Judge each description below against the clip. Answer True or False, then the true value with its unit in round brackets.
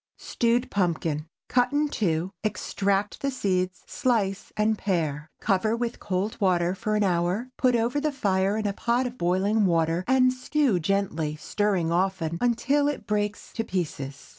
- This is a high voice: True (200 Hz)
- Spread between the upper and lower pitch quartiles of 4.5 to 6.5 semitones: True (4.9 semitones)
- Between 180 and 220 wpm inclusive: False (160 wpm)